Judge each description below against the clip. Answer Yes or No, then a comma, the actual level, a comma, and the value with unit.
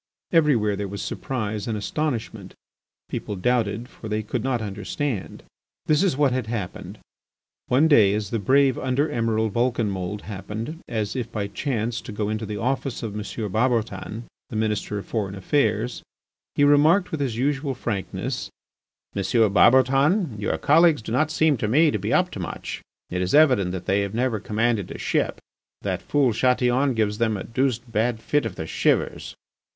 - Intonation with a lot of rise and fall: No, average, 4.2 semitones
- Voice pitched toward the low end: Yes, low, 115 Hz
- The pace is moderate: Yes, average, 175 wpm